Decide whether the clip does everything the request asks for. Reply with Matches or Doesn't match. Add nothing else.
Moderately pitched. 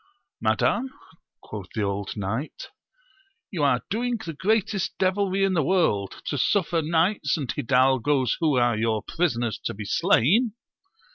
Matches